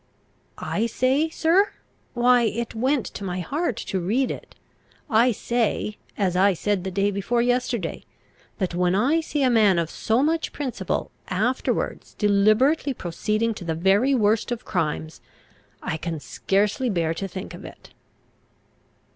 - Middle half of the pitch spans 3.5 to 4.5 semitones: No, average, 4.9 semitones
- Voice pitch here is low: No, high, 215 Hz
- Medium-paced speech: Yes, average, 150 wpm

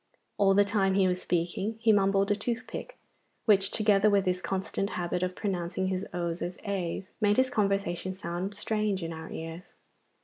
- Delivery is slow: No, average, 175 wpm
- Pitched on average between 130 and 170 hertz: No, high, 195 Hz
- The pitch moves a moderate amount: No, narrow, 2.3 semitones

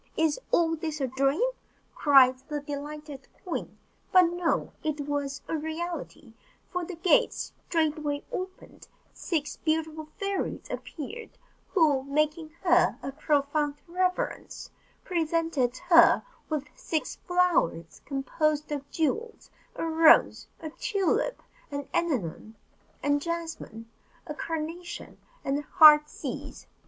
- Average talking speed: No, slow, 115 wpm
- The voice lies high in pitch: Yes, very high, 310 Hz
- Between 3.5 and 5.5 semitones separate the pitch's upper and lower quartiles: No, average, 2.9 semitones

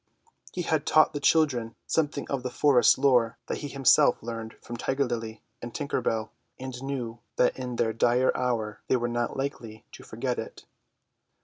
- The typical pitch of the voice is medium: No, low, 125 Hz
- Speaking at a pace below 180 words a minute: No, average, 185 wpm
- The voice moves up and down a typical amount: Yes, average, 3.1 semitones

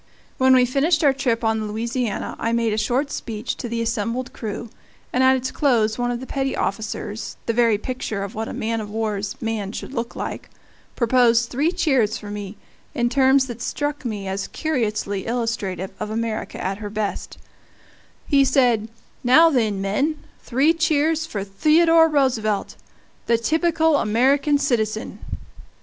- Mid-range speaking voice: No, high, 235 Hz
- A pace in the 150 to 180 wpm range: Yes, average, 165 wpm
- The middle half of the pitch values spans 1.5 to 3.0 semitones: No, average, 4.0 semitones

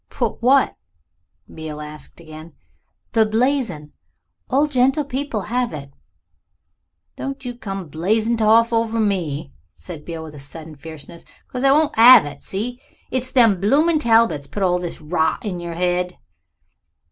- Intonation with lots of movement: Yes, wide, 7.4 semitones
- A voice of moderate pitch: No, high, 205 Hz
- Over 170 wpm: No, average, 145 wpm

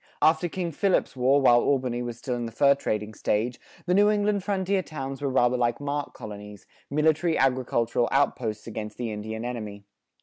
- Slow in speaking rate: No, average, 175 wpm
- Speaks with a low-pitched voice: Yes, low, 130 Hz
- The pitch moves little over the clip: No, average, 5.2 semitones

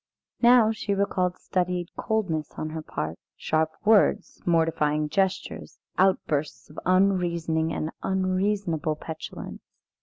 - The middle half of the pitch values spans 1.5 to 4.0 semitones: Yes, average, 3.6 semitones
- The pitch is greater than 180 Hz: No, medium, 175 Hz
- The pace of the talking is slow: Yes, slow, 110 wpm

